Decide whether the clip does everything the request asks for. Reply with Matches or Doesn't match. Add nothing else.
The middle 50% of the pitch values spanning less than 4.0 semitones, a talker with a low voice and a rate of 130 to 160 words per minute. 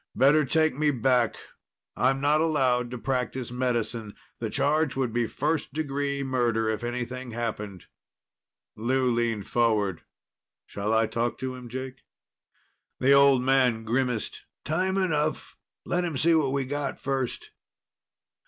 Matches